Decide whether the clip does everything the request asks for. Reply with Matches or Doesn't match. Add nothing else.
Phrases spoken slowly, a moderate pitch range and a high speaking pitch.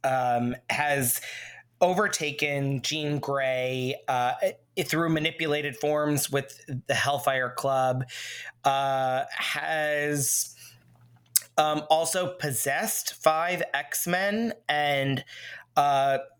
Doesn't match